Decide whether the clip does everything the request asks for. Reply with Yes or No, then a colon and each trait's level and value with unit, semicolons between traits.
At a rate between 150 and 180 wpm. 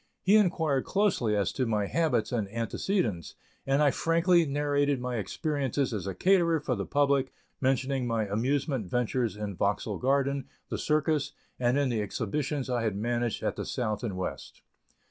Yes: average, 165 wpm